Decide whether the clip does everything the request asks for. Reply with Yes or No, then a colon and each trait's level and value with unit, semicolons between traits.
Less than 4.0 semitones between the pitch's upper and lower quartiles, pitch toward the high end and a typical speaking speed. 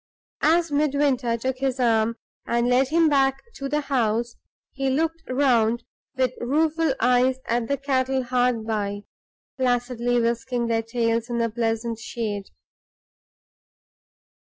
No: average, 2.8 semitones; high, 245 Hz; slow, 130 wpm